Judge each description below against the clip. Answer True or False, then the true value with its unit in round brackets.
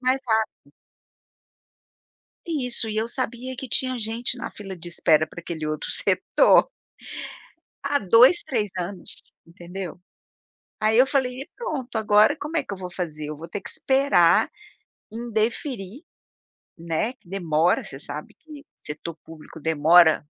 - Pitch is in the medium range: False (215 Hz)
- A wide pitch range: True (7.1 semitones)